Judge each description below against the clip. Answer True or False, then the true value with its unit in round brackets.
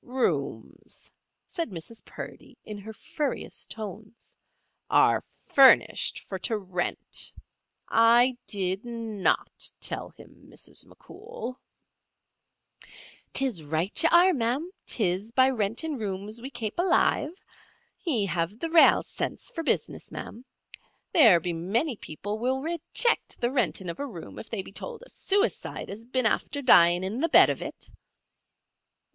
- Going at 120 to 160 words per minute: True (135 wpm)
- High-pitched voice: True (230 Hz)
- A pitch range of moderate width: False (6.3 semitones)